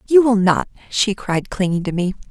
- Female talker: Yes, female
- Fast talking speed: Yes, fast, 210 wpm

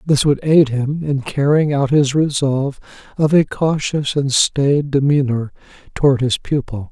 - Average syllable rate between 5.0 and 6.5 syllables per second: No, 4.3 syllables/s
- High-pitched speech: No, medium, 140 Hz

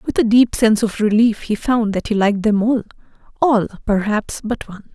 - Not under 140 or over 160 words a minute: No, fast, 205 wpm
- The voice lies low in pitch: No, high, 220 Hz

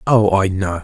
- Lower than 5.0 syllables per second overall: Yes, 4.4 syllables/s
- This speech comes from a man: Yes, male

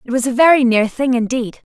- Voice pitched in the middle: No, very high, 250 Hz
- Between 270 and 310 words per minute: No, fast, 240 wpm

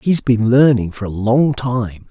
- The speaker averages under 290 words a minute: Yes, average, 200 wpm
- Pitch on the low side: Yes, low, 120 Hz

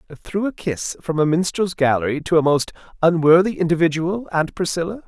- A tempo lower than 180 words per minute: Yes, average, 155 wpm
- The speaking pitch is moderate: Yes, medium, 170 Hz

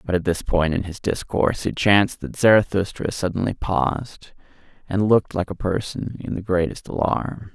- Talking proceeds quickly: No, average, 175 wpm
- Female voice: No, male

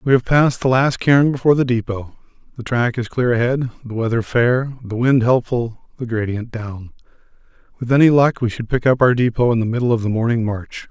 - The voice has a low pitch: Yes, low, 120 Hz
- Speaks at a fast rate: Yes, fast, 210 wpm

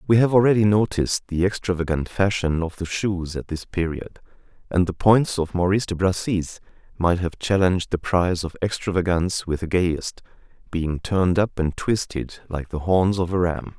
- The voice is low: Yes, very low, 90 Hz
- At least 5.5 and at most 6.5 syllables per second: No, 5.1 syllables/s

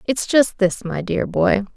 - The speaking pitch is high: Yes, high, 210 Hz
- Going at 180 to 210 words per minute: Yes, fast, 205 wpm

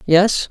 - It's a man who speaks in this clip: No, female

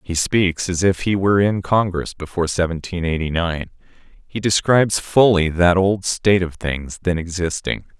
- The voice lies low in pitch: Yes, very low, 90 Hz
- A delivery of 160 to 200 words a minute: Yes, average, 165 wpm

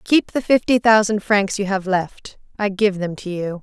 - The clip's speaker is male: No, female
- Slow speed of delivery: No, average, 200 wpm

